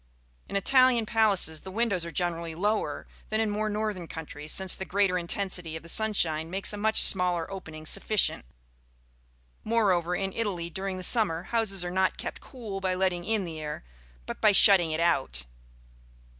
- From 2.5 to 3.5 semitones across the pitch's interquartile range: No, average, 3.9 semitones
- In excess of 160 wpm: Yes, average, 170 wpm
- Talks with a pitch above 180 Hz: Yes, high, 190 Hz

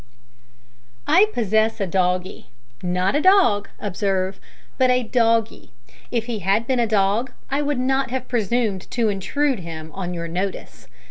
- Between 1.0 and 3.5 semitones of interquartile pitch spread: No, average, 4.8 semitones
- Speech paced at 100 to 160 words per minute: Yes, average, 150 wpm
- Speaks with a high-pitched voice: Yes, high, 220 Hz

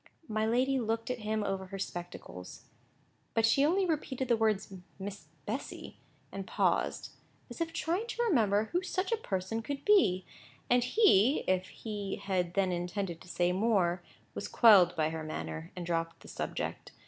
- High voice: Yes, high, 205 Hz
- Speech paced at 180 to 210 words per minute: No, average, 170 wpm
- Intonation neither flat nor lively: No, wide, 5.7 semitones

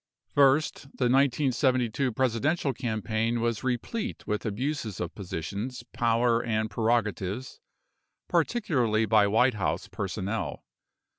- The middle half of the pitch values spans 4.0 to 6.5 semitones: No, average, 3.3 semitones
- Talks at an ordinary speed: No, slow, 100 wpm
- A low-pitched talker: Yes, low, 120 Hz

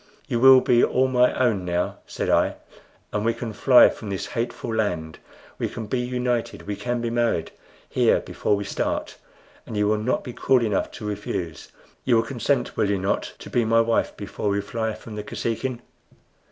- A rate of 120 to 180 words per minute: No, average, 195 wpm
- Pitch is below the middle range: Yes, low, 115 Hz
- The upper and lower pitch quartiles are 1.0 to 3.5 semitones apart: Yes, average, 3.0 semitones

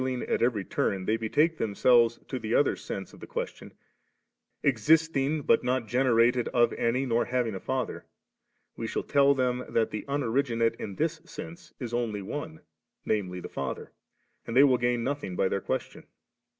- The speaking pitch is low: Yes, low, 120 Hz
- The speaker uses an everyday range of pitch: Yes, average, 3.5 semitones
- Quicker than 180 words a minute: Yes, average, 190 wpm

